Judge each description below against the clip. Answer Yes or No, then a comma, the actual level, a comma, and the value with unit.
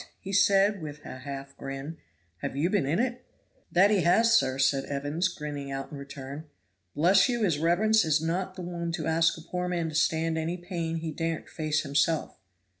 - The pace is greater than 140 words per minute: Yes, average, 195 wpm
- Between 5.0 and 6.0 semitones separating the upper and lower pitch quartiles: No, average, 3.7 semitones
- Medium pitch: Yes, medium, 165 Hz